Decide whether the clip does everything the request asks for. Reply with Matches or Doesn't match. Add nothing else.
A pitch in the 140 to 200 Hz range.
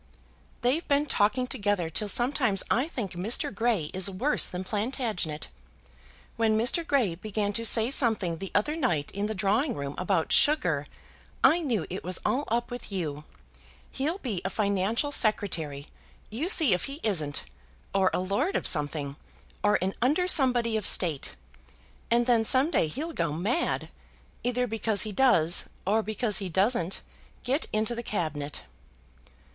Doesn't match